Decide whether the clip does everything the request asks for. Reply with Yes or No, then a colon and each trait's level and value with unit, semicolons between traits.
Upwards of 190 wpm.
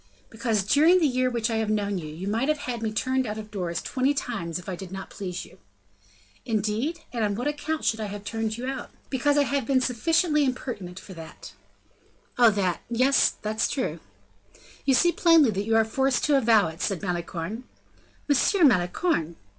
Yes: average, 200 wpm